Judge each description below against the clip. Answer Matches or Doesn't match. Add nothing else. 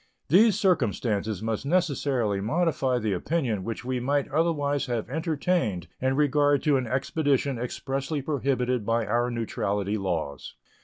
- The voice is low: Matches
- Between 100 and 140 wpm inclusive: Matches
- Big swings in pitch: Doesn't match